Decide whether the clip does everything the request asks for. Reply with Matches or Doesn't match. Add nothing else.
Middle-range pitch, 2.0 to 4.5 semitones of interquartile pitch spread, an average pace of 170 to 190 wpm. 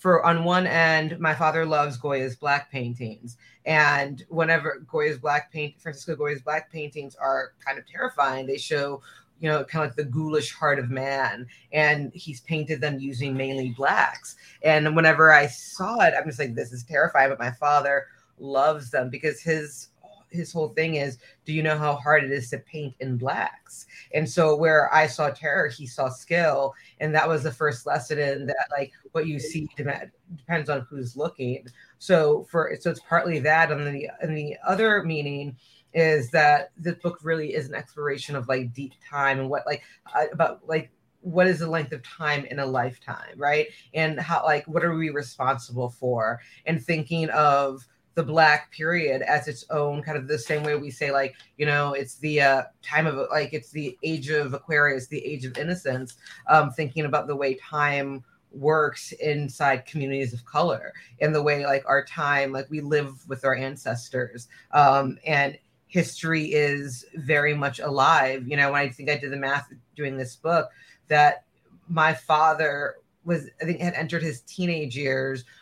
Matches